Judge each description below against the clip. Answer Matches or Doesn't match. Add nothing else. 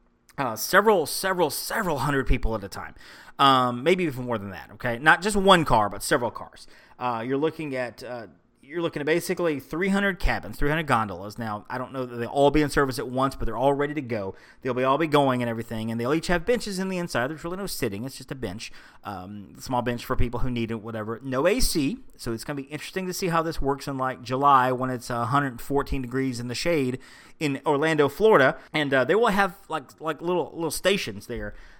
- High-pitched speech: Doesn't match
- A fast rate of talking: Matches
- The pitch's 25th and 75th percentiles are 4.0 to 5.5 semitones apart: Matches